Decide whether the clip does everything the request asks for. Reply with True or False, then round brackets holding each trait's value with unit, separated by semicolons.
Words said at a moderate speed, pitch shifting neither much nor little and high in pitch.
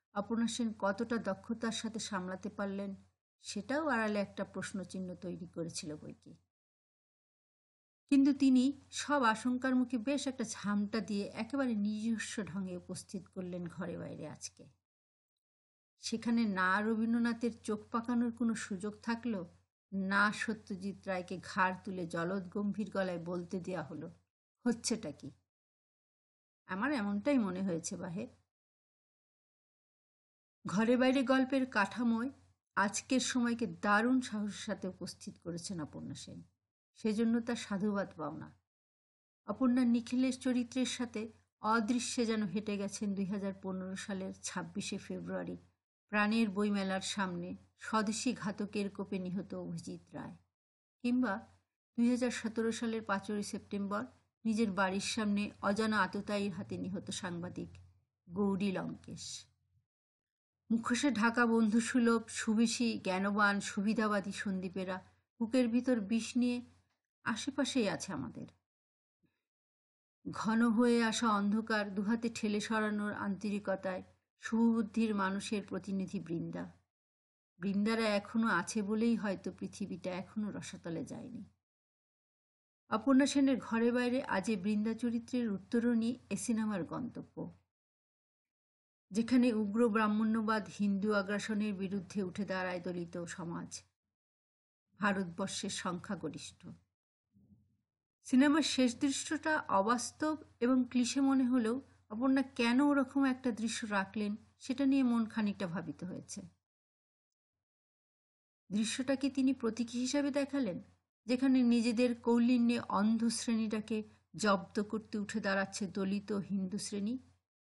True (95 wpm; 3.9 semitones; 210 Hz)